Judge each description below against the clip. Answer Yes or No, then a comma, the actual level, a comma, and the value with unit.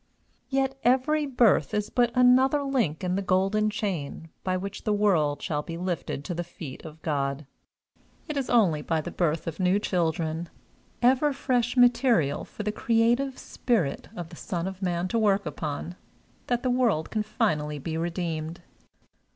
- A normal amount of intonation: No, wide, 6.9 semitones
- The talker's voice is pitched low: No, high, 190 Hz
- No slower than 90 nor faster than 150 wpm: No, average, 165 wpm